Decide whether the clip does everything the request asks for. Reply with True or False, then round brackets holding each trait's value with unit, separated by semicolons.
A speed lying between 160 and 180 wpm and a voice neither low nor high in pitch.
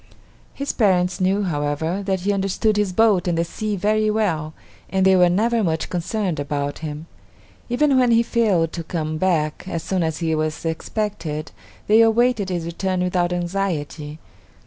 True (170 wpm; 180 Hz)